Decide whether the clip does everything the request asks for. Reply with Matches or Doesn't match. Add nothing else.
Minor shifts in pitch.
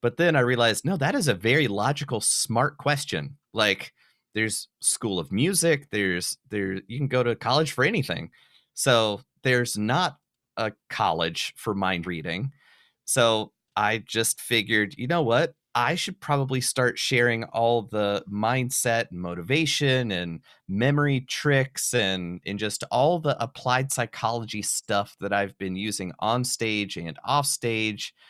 Doesn't match